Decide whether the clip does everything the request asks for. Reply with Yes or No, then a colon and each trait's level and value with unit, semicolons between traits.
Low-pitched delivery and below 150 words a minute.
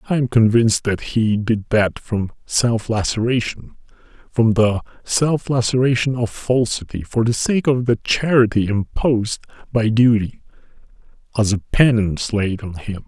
Yes: low, 115 Hz; average, 140 wpm